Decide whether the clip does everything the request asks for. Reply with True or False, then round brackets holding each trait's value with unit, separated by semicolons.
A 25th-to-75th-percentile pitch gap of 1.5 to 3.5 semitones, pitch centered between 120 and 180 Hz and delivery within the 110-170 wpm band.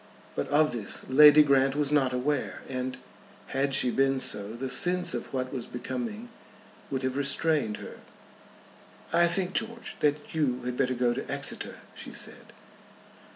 True (3.0 semitones; 135 Hz; 155 wpm)